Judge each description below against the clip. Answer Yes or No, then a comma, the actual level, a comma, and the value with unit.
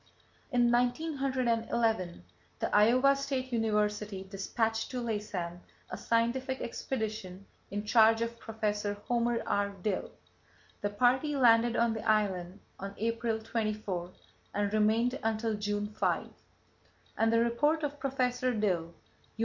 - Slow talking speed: Yes, slow, 125 wpm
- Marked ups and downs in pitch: No, average, 2.7 semitones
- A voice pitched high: Yes, high, 225 Hz